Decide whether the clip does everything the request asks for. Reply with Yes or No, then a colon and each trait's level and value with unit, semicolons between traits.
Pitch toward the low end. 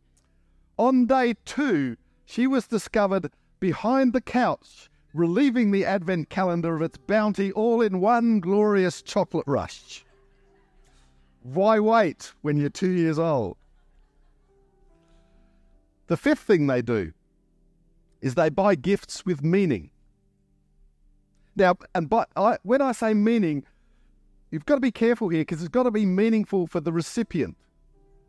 No: medium, 175 Hz